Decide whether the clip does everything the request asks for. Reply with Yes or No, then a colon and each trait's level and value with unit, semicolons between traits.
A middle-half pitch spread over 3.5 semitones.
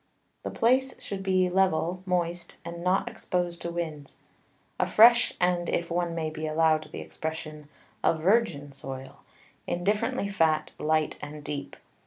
No: average, 3.2 semitones